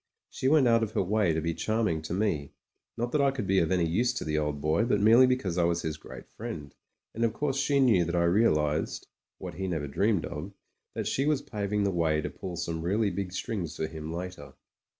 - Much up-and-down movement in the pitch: Yes, wide, 5.8 semitones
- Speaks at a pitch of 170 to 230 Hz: No, very low, 95 Hz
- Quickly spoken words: Yes, fast, 245 wpm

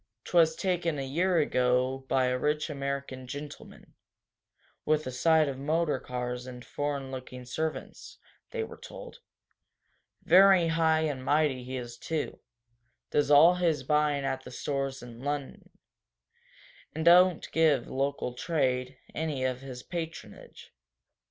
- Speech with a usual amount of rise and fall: Yes, average, 3.7 semitones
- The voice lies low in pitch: No, medium, 145 Hz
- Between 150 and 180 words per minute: No, slow, 135 wpm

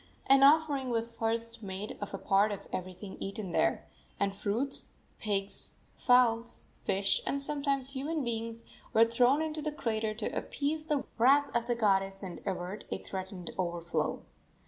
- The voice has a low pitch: No, high, 230 Hz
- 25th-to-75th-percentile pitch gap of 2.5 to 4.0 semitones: No, wide, 5.6 semitones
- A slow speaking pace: No, average, 155 wpm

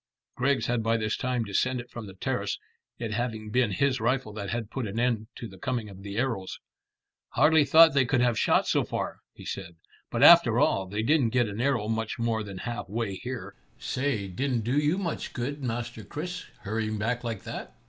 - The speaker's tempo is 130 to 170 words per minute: No, fast, 205 wpm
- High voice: No, low, 115 Hz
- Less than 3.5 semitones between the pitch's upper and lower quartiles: Yes, average, 3.0 semitones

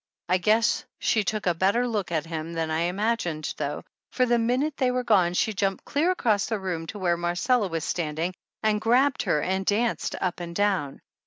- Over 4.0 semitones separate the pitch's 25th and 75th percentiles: Yes, average, 5.1 semitones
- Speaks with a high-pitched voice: Yes, high, 195 Hz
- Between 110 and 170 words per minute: No, average, 200 wpm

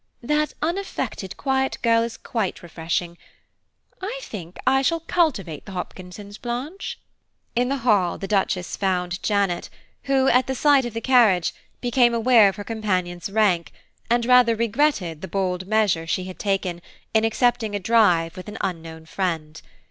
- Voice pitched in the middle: No, high, 210 Hz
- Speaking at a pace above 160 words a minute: No, average, 155 wpm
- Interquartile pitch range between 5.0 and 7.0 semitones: Yes, average, 5.3 semitones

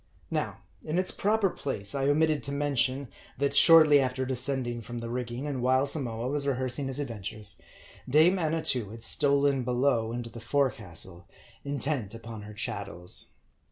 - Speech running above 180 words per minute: No, average, 155 wpm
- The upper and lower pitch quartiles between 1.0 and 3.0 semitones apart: No, average, 3.6 semitones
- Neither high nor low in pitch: No, low, 130 Hz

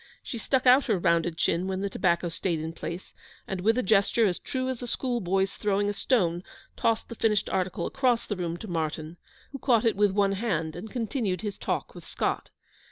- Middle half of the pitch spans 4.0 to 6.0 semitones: Yes, average, 4.7 semitones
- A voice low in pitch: No, high, 195 Hz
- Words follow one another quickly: Yes, fast, 215 wpm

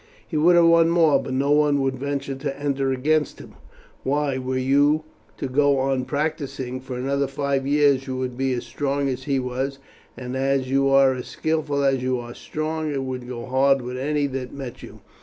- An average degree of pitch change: No, narrow, 1.8 semitones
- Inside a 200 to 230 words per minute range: Yes, fast, 205 wpm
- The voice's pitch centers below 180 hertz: Yes, low, 135 Hz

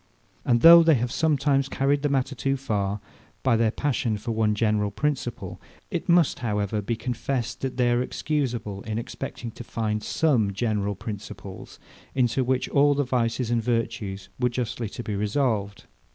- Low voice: Yes, low, 120 Hz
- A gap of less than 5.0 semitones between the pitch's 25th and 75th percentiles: Yes, average, 4.1 semitones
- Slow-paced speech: No, average, 170 wpm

